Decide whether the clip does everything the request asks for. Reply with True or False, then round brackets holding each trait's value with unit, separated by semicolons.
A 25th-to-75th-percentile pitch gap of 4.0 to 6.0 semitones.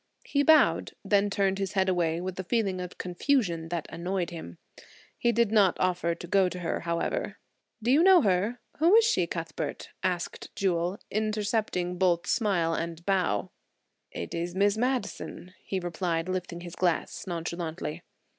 False (3.2 semitones)